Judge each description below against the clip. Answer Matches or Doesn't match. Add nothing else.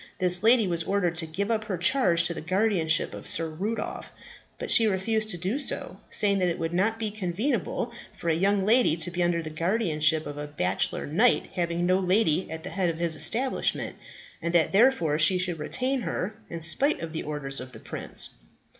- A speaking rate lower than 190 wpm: Doesn't match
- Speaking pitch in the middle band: Matches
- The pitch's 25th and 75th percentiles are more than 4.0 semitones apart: Matches